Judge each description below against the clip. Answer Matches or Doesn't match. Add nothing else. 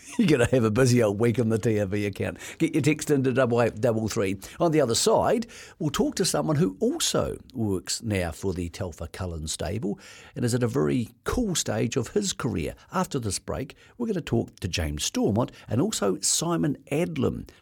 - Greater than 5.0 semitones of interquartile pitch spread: Matches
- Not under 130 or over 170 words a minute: Doesn't match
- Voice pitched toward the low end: Matches